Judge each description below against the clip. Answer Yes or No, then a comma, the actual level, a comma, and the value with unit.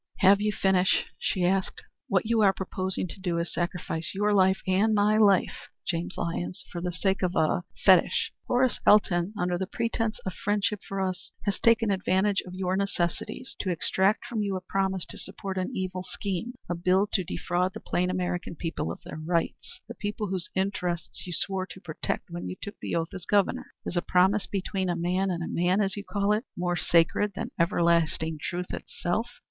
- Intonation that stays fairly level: Yes, narrow, 2.2 semitones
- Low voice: No, medium, 185 Hz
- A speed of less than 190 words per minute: No, average, 195 wpm